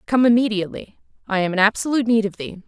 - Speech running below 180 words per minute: No, average, 200 wpm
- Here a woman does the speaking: Yes, female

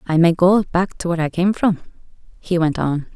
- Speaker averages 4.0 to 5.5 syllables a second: Yes, 5.4 syllables/s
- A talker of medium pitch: Yes, medium, 175 Hz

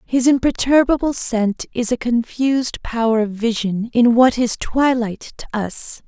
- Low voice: No, high, 240 Hz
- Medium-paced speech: Yes, average, 150 wpm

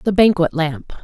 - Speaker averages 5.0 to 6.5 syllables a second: No, 4.2 syllables/s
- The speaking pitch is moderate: Yes, medium, 170 Hz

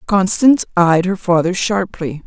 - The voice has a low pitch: No, medium, 185 Hz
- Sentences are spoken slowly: Yes, slow, 130 wpm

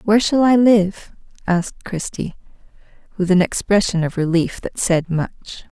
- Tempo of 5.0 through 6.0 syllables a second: No, 4.5 syllables/s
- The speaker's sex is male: No, female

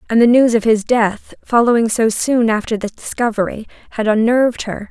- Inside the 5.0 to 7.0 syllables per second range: Yes, 5.3 syllables/s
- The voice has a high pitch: Yes, high, 225 Hz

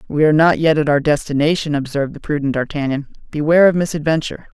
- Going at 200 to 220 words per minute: No, average, 185 wpm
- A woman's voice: No, male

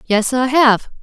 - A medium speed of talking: Yes, average, 175 wpm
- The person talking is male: No, female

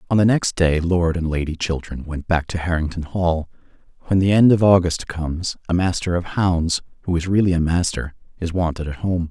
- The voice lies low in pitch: Yes, very low, 85 Hz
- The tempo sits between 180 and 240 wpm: Yes, average, 195 wpm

